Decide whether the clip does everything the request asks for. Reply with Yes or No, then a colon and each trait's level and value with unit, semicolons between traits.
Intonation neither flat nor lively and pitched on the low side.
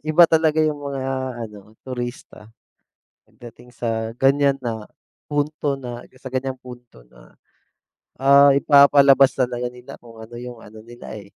Yes: average, 3.1 semitones; low, 125 Hz